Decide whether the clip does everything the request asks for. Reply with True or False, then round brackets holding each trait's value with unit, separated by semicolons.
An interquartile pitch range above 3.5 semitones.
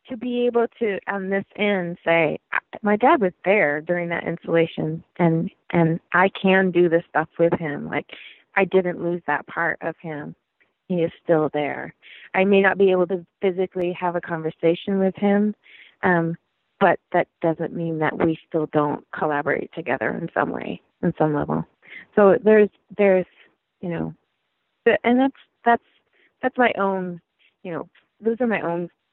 False (3.2 semitones)